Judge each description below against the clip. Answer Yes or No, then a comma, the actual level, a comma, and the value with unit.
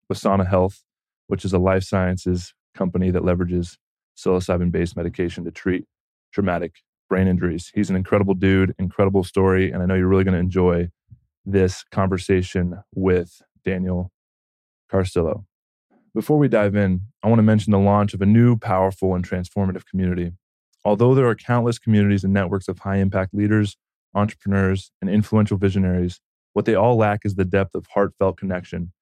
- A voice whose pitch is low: Yes, very low, 95 Hz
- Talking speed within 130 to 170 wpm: Yes, average, 165 wpm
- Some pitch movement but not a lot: No, narrow, 2.0 semitones